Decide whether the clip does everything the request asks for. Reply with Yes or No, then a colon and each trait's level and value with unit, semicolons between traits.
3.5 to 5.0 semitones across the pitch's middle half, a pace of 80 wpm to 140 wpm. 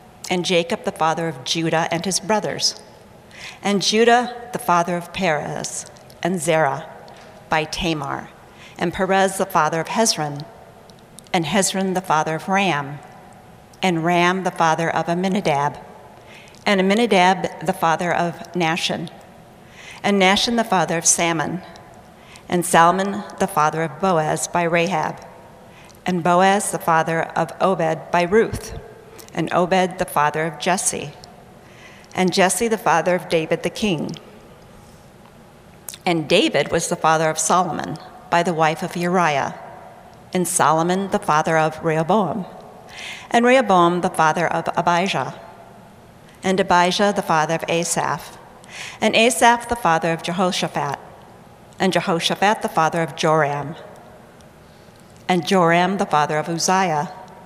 No: average, 2.7 semitones; slow, 135 wpm